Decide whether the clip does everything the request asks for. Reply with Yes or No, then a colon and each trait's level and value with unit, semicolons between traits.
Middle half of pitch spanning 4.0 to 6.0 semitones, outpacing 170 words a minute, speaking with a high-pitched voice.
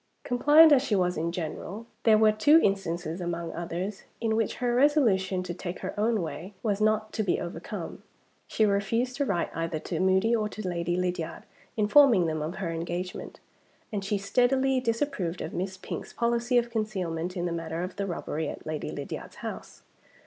Yes: average, 4.9 semitones; average, 185 wpm; high, 195 Hz